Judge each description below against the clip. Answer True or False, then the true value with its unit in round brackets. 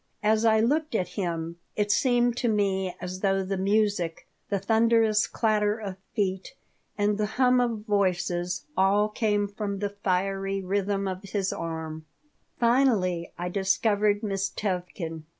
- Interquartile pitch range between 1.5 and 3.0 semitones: True (2.6 semitones)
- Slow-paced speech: False (145 wpm)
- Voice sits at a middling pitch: False (200 Hz)